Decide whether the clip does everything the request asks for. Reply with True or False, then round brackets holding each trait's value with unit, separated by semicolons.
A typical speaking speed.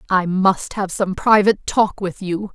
True (190 wpm)